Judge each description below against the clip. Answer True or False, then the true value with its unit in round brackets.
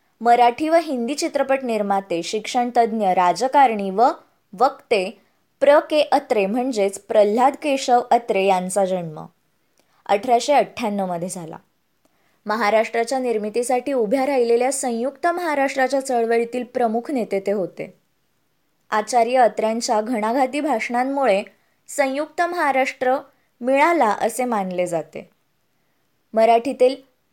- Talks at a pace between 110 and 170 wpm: False (95 wpm)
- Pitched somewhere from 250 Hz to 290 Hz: False (240 Hz)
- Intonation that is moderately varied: True (4.3 semitones)